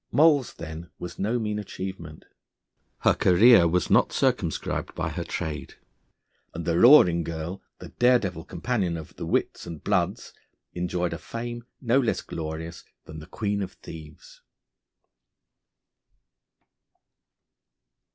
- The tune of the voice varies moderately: No, wide, 5.7 semitones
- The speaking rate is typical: No, slow, 120 wpm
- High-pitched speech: No, very low, 90 Hz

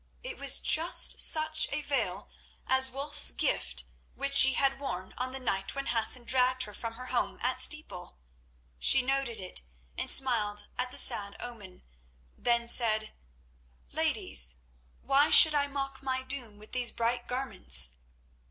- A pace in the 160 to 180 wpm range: No, average, 150 wpm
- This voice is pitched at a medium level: No, very high, 255 Hz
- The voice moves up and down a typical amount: Yes, average, 3.8 semitones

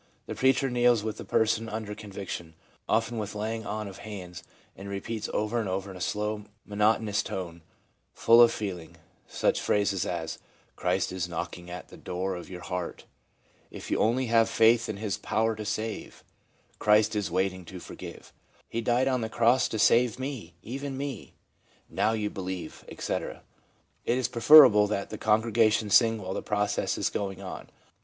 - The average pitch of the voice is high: No, low, 105 Hz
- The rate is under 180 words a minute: No, average, 185 wpm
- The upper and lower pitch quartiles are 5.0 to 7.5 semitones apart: No, average, 2.9 semitones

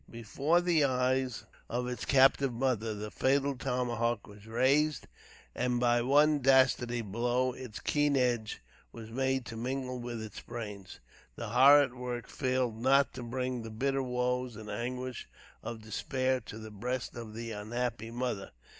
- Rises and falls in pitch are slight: Yes, narrow, 2.3 semitones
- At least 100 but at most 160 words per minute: Yes, average, 155 wpm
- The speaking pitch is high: No, low, 125 Hz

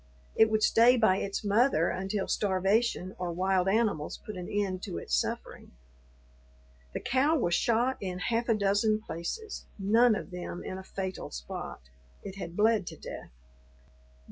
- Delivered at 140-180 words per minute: Yes, average, 160 wpm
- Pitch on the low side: No, high, 200 Hz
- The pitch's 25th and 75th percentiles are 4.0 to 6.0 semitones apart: No, average, 3.4 semitones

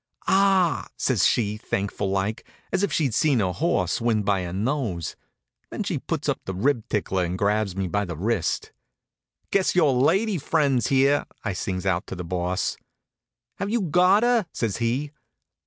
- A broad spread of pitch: Yes, wide, 8.3 semitones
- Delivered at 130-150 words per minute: No, average, 180 wpm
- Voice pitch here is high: No, low, 115 Hz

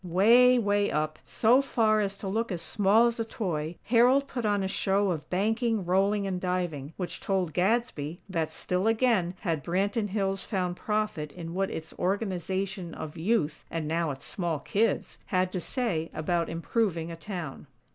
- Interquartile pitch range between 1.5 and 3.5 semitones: No, average, 4.3 semitones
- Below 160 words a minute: No, average, 175 wpm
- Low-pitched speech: No, high, 190 Hz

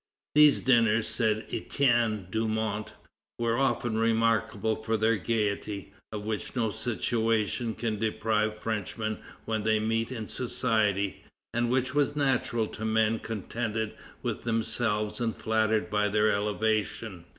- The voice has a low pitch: Yes, low, 110 Hz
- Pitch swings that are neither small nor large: No, narrow, 1.2 semitones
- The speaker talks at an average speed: No, slow, 130 wpm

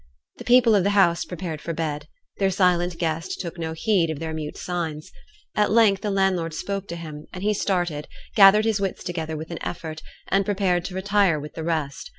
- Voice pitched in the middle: Yes, medium, 175 Hz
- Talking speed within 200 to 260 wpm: Yes, fast, 205 wpm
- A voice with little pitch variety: No, average, 3.5 semitones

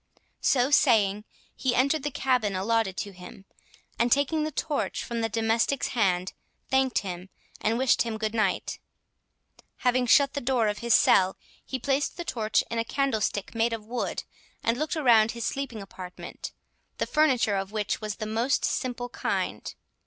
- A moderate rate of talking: Yes, average, 170 wpm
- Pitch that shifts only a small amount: No, average, 3.8 semitones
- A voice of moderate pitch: No, high, 230 Hz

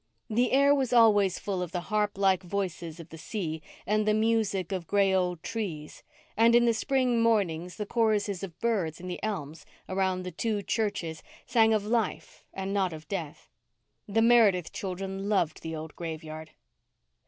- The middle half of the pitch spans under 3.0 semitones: No, average, 4.0 semitones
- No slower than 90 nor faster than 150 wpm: No, average, 175 wpm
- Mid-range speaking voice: No, high, 195 Hz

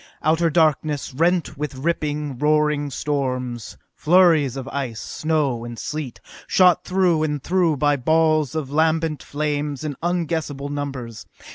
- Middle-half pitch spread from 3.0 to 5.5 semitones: No, narrow, 2.5 semitones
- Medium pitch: Yes, medium, 150 Hz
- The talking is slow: Yes, slow, 130 wpm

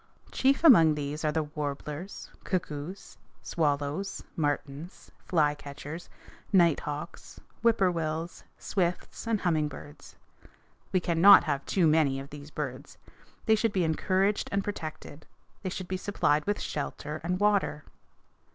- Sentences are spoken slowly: Yes, slow, 125 wpm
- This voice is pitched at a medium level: Yes, medium, 160 Hz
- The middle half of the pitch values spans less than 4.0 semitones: No, average, 4.3 semitones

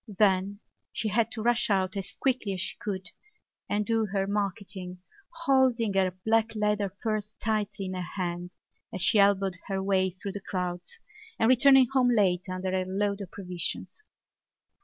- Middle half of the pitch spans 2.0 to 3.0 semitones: Yes, narrow, 2.5 semitones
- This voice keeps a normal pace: Yes, average, 165 wpm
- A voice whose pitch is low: No, high, 200 Hz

